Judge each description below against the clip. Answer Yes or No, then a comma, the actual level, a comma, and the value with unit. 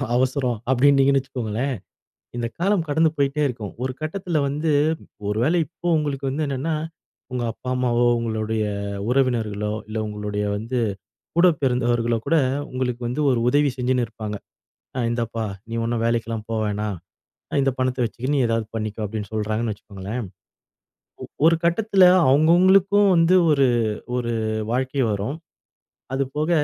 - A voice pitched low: Yes, low, 125 Hz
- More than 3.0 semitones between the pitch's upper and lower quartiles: Yes, average, 4.3 semitones